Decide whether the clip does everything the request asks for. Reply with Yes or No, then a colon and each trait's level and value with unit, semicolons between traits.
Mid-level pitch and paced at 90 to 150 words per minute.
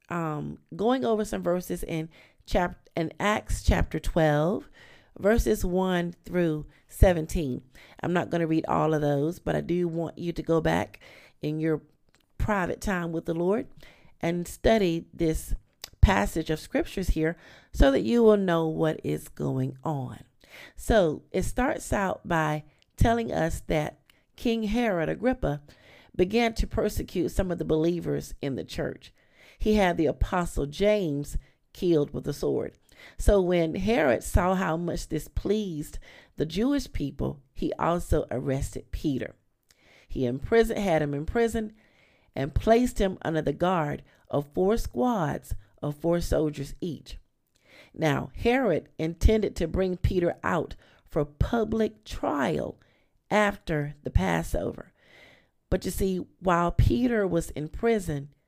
Yes: medium, 165 Hz; average, 145 wpm